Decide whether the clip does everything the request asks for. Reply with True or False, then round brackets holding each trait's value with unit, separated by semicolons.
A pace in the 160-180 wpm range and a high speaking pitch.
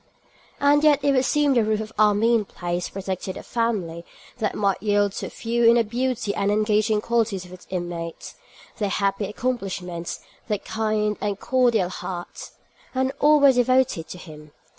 True (165 wpm; 210 Hz)